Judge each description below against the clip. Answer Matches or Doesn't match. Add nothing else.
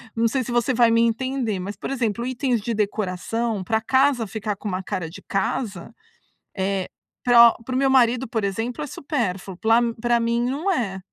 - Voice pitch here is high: Matches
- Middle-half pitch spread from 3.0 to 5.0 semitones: Matches